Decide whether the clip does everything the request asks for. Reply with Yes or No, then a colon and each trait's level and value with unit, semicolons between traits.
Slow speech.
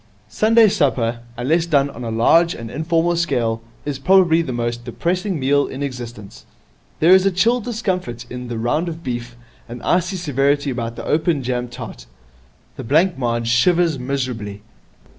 No: average, 160 wpm